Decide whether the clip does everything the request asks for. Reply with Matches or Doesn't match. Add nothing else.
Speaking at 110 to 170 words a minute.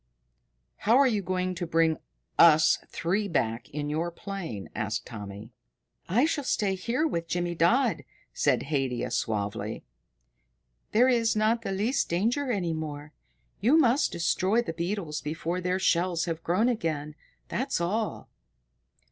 Matches